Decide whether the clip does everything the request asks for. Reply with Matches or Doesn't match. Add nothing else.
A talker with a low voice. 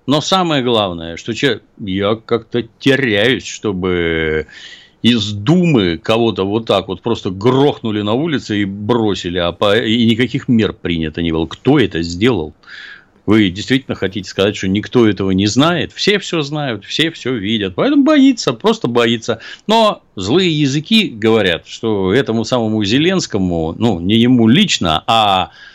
Matches